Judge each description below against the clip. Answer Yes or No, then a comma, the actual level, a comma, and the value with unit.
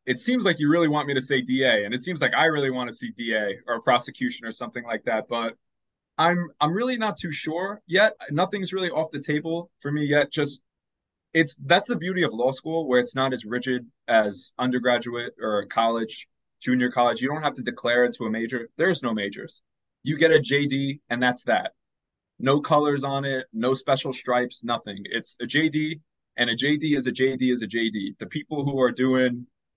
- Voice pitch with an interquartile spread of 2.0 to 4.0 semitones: No, average, 4.4 semitones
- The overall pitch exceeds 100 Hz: Yes, low, 135 Hz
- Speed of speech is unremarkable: No, fast, 210 wpm